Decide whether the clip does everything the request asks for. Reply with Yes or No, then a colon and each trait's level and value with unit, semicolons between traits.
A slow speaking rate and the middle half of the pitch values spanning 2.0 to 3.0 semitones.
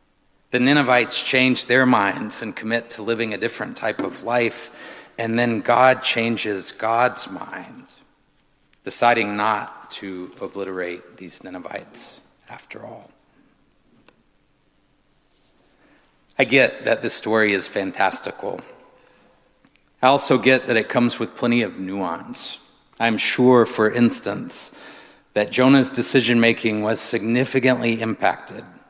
Yes: slow, 115 wpm; average, 2.7 semitones